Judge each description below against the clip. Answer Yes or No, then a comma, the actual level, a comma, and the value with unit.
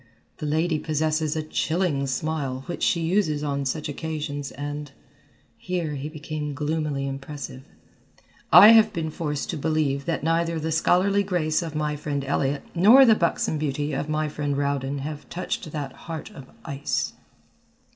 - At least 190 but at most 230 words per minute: No, average, 155 wpm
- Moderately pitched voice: Yes, medium, 155 Hz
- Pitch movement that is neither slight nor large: No, narrow, 2.3 semitones